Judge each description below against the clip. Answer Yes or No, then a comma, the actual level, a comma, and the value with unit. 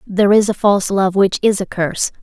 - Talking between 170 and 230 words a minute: No, fast, 245 wpm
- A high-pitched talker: Yes, high, 195 Hz